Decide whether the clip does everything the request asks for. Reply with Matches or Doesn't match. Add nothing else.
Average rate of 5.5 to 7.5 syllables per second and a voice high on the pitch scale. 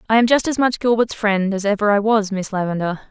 Matches